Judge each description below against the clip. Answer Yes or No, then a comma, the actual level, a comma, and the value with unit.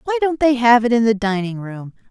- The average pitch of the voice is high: Yes, high, 235 Hz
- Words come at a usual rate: No, fast, 255 wpm